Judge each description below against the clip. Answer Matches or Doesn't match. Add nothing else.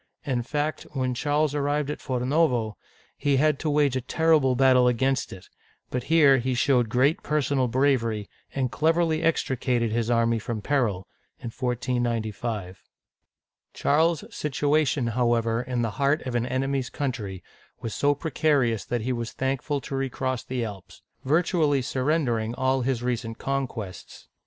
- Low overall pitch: Matches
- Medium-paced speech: Matches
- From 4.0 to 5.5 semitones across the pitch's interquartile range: Doesn't match